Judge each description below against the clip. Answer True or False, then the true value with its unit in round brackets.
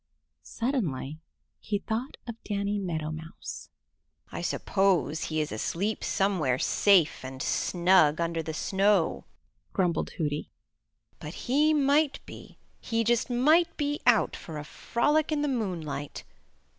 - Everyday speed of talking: False (130 wpm)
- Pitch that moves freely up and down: True (7.3 semitones)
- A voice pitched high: True (195 Hz)